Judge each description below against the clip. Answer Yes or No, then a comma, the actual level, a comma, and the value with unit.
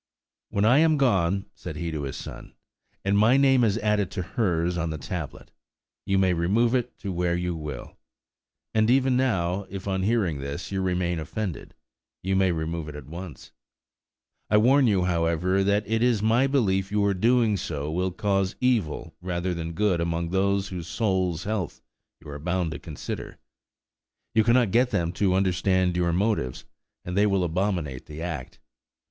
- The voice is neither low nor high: No, very low, 95 Hz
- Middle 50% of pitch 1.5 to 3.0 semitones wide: No, average, 3.9 semitones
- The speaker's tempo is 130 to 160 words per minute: No, average, 175 wpm